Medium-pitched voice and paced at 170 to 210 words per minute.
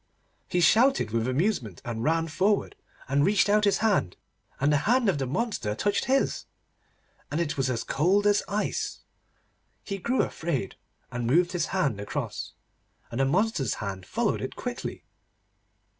No: medium, 165 Hz; average, 160 wpm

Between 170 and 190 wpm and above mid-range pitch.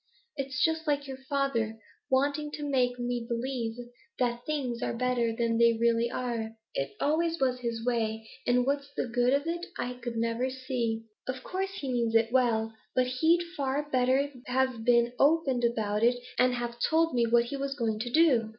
Yes: average, 185 wpm; very high, 250 Hz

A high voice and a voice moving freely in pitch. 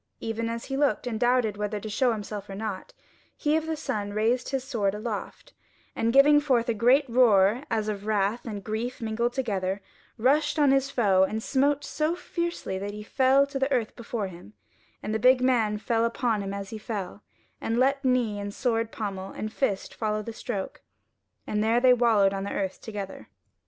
No: high, 225 Hz; average, 3.7 semitones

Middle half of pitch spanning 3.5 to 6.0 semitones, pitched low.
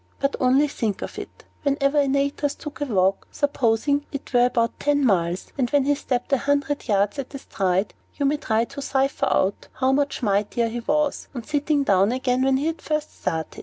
No: average, 4.1 semitones; very high, 270 Hz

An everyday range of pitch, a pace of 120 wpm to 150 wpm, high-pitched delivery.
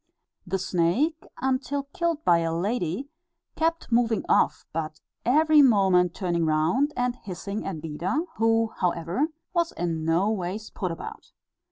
No: wide, 7.5 semitones; average, 140 wpm; high, 200 Hz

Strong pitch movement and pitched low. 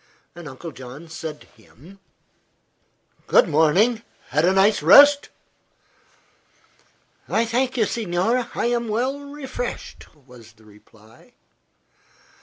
No: wide, 8.7 semitones; medium, 185 Hz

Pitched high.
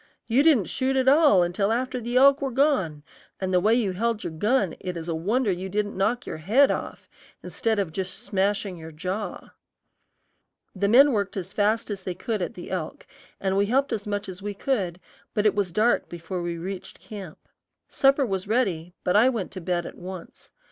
Yes: high, 200 Hz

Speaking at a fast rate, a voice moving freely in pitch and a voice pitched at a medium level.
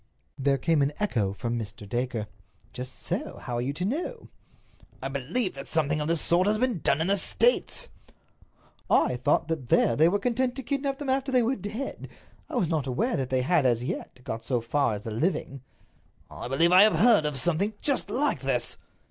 Yes: fast, 210 wpm; wide, 9.0 semitones; medium, 155 Hz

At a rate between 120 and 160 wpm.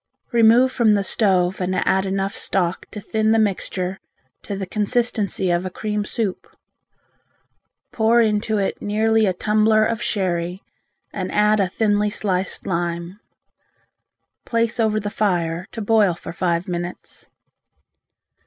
Yes: slow, 135 wpm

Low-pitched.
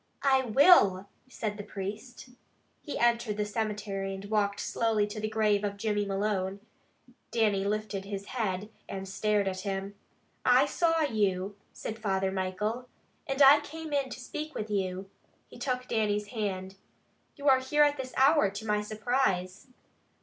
No: high, 210 Hz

